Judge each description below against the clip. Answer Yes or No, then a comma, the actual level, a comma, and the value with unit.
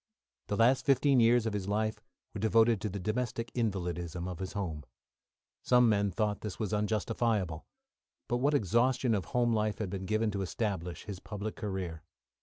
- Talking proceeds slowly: No, average, 175 wpm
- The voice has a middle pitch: No, low, 105 Hz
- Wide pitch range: No, average, 3.4 semitones